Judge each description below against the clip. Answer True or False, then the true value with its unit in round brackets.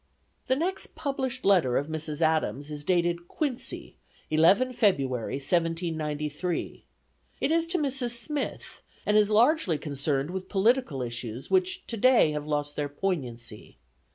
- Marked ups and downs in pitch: True (9.0 semitones)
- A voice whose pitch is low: False (170 Hz)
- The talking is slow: True (130 wpm)